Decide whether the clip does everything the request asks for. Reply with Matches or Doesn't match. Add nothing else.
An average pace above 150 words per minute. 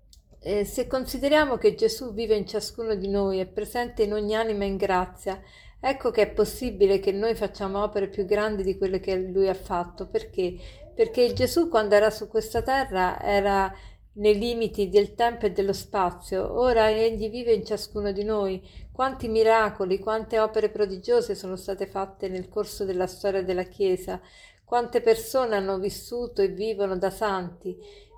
Matches